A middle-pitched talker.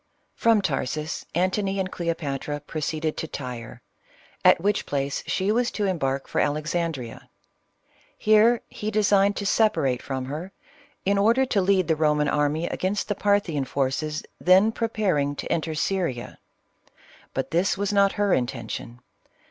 Yes: medium, 170 Hz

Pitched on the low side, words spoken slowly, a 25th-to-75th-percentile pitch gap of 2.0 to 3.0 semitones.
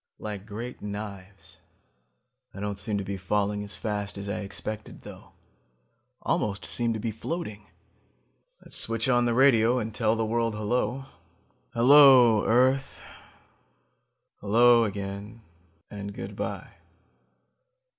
Yes: low, 110 Hz; slow, 125 wpm; narrow, 2.6 semitones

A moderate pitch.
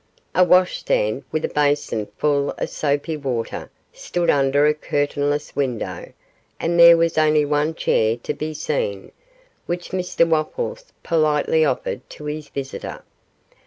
Yes: medium, 150 Hz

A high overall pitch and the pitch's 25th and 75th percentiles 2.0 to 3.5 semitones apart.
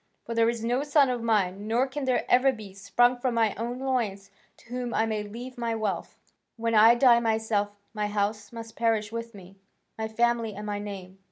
Yes: high, 225 Hz; narrow, 2.5 semitones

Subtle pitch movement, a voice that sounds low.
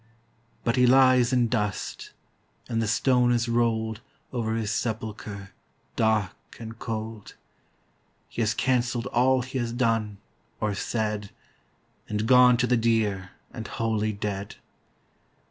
Yes: narrow, 2.3 semitones; low, 115 Hz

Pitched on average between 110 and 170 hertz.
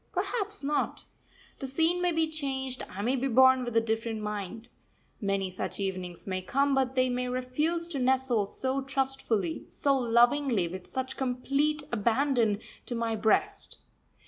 No: very high, 255 Hz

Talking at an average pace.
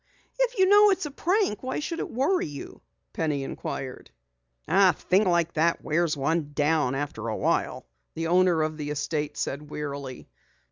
Yes: average, 160 wpm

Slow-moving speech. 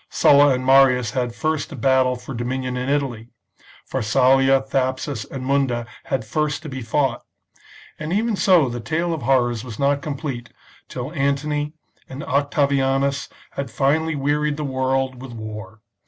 No: average, 155 wpm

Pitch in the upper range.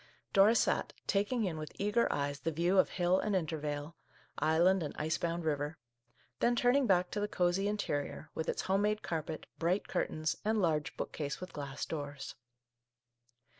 No: medium, 170 Hz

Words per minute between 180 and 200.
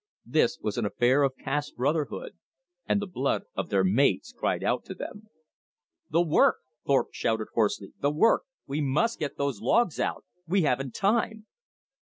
No: average, 165 wpm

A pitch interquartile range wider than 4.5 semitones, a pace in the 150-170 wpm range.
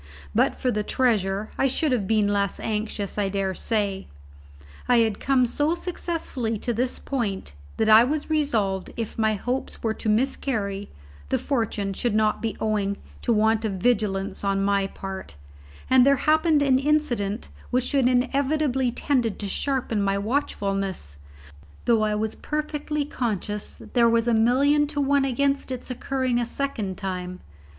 Yes: average, 4.9 semitones; average, 160 wpm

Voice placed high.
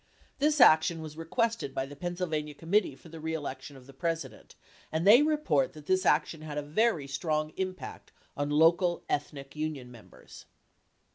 No: medium, 155 Hz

